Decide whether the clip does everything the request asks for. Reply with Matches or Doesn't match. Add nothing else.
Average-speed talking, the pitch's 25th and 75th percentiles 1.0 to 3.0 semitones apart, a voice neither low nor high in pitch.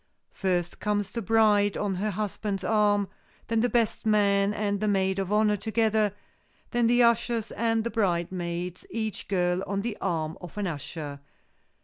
Doesn't match